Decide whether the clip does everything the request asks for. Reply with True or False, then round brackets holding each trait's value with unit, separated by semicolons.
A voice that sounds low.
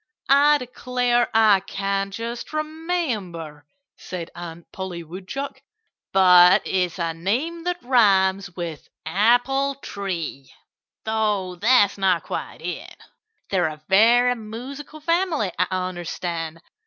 False (200 Hz)